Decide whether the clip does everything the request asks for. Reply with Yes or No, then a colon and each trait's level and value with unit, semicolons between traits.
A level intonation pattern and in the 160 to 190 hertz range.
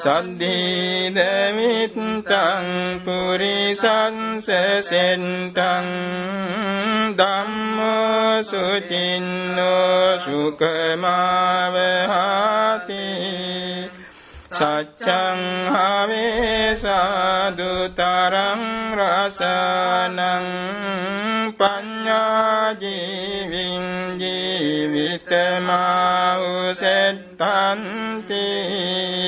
Yes: narrow, 1.8 semitones; medium, 185 Hz